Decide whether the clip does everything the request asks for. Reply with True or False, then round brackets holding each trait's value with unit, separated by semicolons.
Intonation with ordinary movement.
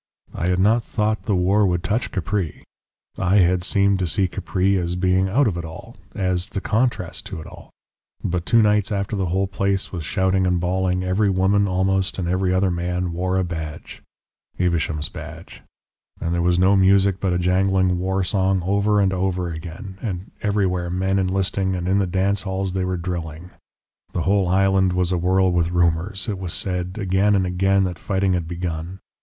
False (1.6 semitones)